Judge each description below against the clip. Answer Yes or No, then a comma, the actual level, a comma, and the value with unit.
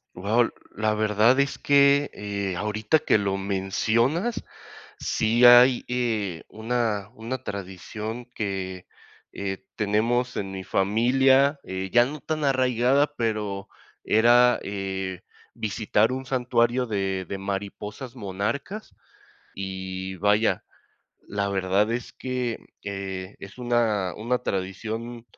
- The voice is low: Yes, low, 110 Hz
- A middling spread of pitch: Yes, average, 3.9 semitones